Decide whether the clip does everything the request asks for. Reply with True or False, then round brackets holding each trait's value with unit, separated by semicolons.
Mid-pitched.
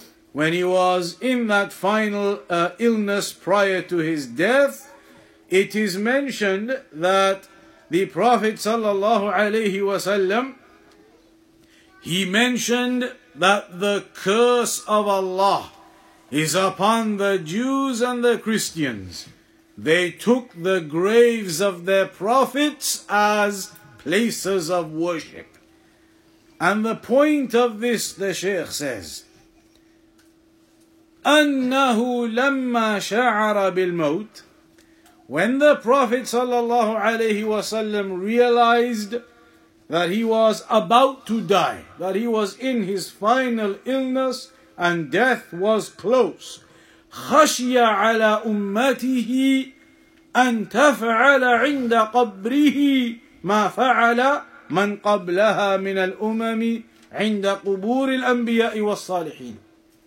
False (225 Hz)